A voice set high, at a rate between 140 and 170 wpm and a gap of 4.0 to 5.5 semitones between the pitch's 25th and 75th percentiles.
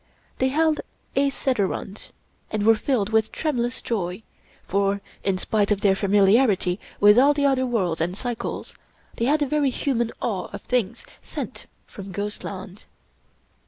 Yes: high, 220 Hz; average, 150 wpm; average, 4.8 semitones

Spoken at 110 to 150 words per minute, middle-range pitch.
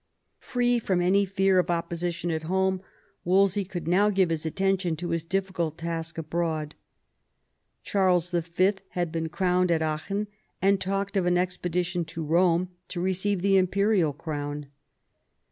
Yes: average, 145 wpm; medium, 180 Hz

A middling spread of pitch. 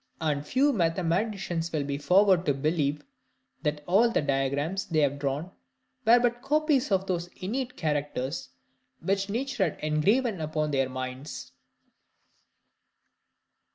No: wide, 5.9 semitones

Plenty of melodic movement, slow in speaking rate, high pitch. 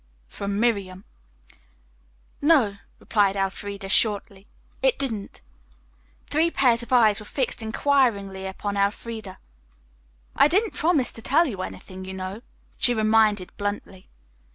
No: average, 4.0 semitones; slow, 120 wpm; high, 210 Hz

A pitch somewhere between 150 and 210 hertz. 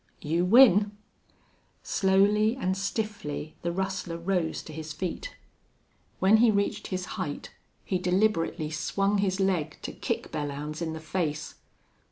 Yes: medium, 185 Hz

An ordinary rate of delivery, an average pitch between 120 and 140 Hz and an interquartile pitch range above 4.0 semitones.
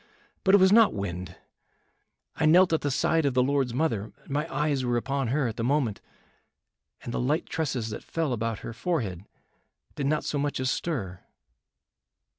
Yes: average, 180 wpm; low, 135 Hz; average, 5.1 semitones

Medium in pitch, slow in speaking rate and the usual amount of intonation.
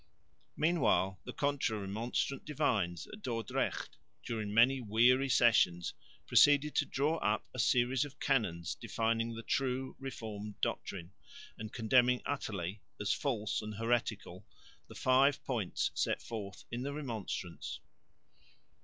No: low, 115 Hz; slow, 125 wpm; average, 4.2 semitones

